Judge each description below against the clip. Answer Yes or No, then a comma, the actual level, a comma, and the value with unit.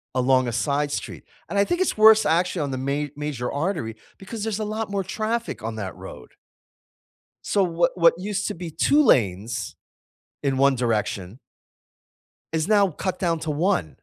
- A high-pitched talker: No, medium, 160 Hz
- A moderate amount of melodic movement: No, wide, 7.7 semitones